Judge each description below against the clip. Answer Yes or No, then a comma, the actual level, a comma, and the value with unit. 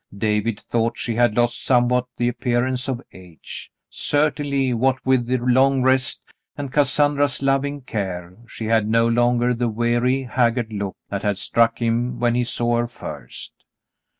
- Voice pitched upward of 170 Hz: No, low, 120 Hz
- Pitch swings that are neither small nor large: No, narrow, 2.1 semitones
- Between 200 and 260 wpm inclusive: No, average, 155 wpm